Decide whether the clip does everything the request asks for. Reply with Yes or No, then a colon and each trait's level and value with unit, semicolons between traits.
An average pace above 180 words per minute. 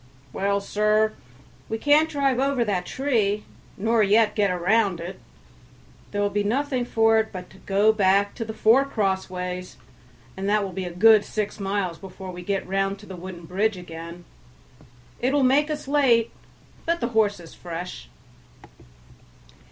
No: average, 165 wpm